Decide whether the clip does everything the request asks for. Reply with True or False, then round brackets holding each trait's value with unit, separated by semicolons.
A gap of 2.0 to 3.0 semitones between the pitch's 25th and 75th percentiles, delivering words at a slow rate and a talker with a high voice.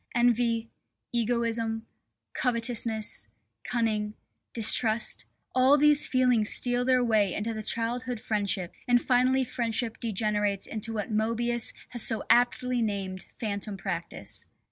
True (2.4 semitones; 115 wpm; 230 Hz)